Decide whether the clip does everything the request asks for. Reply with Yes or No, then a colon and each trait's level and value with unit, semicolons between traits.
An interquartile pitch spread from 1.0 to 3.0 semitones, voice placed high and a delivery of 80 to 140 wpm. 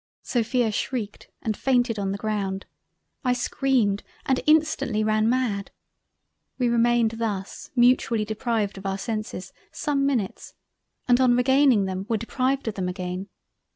No: average, 3.9 semitones; high, 225 Hz; slow, 135 wpm